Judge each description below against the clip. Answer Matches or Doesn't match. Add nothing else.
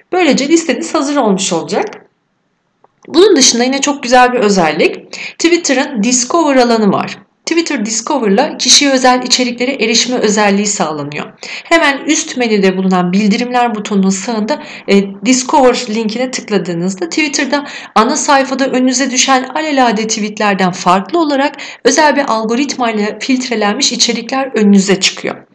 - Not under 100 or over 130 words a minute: Matches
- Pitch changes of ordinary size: Matches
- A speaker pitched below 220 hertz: Doesn't match